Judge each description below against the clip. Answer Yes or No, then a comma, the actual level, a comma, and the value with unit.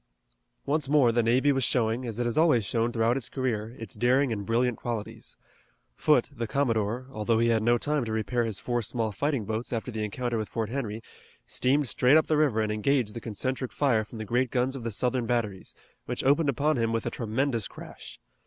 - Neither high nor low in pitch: No, low, 120 Hz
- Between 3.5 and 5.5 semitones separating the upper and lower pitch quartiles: No, average, 2.8 semitones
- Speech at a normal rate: No, fast, 220 wpm